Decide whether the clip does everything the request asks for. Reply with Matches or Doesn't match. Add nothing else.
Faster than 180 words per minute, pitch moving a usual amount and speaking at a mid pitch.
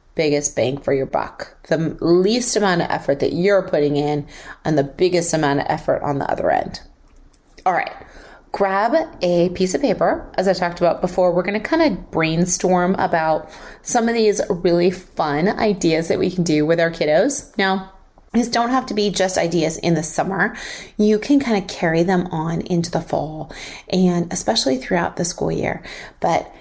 Matches